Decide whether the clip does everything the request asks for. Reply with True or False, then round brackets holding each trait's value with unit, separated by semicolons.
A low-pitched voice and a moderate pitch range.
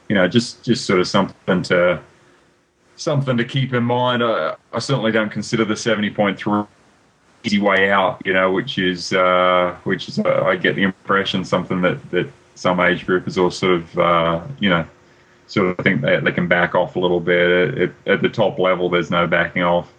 True (95 Hz; 3.8 semitones)